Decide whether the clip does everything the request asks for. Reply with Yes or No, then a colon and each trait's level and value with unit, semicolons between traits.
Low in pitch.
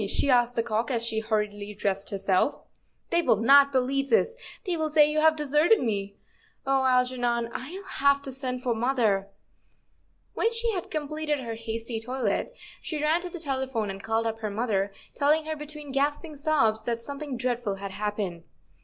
No: very high, 255 Hz